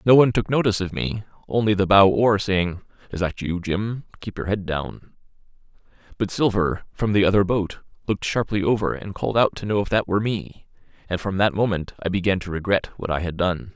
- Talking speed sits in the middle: No, fast, 215 wpm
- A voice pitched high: No, low, 100 Hz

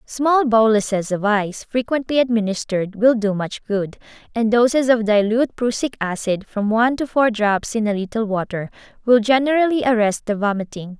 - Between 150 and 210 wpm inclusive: Yes, average, 165 wpm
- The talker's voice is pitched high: Yes, high, 225 Hz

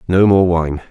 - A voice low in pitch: Yes, very low, 90 Hz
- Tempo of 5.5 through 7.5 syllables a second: No, 4.4 syllables/s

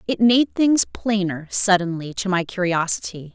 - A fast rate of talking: No, average, 145 wpm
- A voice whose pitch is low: No, high, 195 Hz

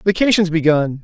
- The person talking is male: Yes, male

